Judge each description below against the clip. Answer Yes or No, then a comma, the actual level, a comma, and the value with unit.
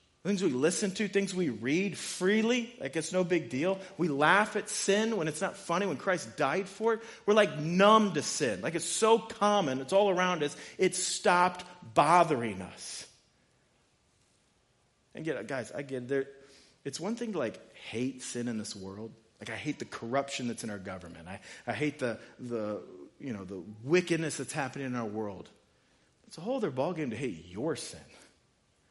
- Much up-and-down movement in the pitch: Yes, wide, 7.6 semitones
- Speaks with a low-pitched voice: No, medium, 165 Hz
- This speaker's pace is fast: No, average, 185 wpm